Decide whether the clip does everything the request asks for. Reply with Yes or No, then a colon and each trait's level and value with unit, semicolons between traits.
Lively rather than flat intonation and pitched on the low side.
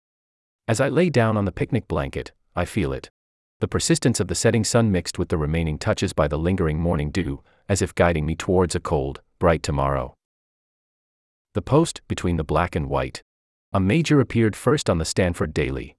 Yes: wide, 5.8 semitones; very low, 90 Hz